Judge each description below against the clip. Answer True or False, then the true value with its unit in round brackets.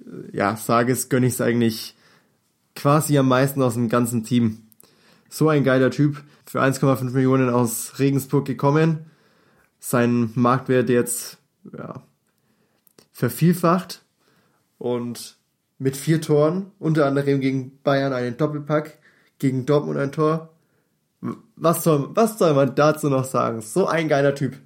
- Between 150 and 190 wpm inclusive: False (135 wpm)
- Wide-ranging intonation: False (3.7 semitones)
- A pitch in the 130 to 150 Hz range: True (135 Hz)